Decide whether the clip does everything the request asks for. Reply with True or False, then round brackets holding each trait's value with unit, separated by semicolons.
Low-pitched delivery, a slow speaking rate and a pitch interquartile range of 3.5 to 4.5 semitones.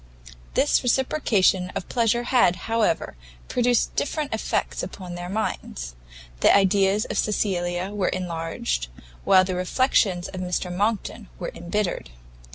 False (195 Hz; 125 wpm; 3.8 semitones)